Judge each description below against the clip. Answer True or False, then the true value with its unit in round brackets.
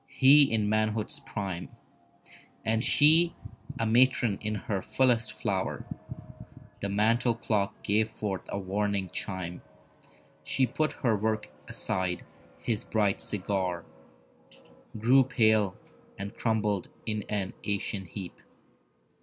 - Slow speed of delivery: True (110 wpm)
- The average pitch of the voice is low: True (105 Hz)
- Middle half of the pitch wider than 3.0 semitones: False (2.6 semitones)